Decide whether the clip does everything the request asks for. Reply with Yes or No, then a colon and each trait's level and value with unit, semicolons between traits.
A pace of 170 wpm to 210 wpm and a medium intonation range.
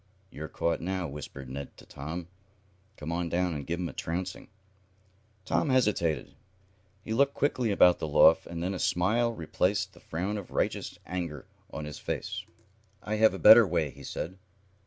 Yes: average, 175 wpm; average, 4.1 semitones